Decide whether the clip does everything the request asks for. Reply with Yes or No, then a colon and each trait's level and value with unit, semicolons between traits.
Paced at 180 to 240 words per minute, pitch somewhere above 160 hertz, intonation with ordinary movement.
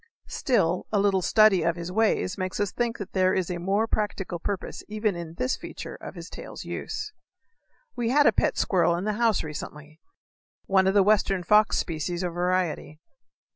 Yes: average, 190 wpm; high, 190 Hz; average, 3.5 semitones